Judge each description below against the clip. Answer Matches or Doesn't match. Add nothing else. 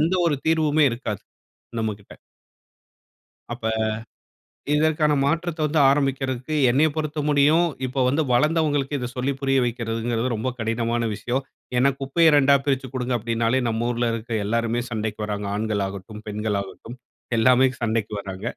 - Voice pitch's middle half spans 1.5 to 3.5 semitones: Doesn't match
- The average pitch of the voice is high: Doesn't match